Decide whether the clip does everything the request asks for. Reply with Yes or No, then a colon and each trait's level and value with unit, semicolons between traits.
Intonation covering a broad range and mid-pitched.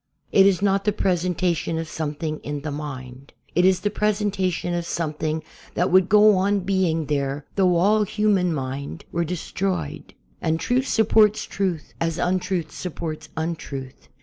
No: average, 4.0 semitones; medium, 175 Hz